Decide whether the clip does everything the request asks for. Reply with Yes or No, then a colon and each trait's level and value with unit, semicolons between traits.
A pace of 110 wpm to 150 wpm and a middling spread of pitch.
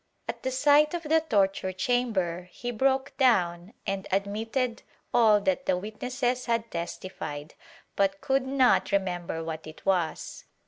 No: average, 140 wpm; wide, 5.8 semitones